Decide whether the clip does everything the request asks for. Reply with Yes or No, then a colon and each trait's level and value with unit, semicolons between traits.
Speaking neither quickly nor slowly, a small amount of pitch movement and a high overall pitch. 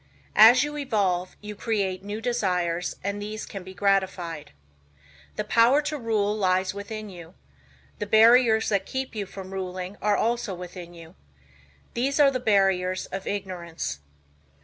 No: average, 150 wpm; average, 3.3 semitones; high, 200 Hz